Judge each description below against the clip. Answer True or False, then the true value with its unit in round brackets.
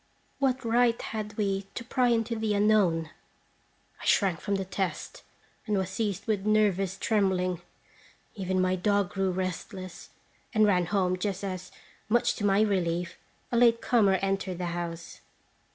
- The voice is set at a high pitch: True (195 Hz)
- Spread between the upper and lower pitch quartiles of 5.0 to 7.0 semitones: False (2.8 semitones)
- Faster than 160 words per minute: False (150 wpm)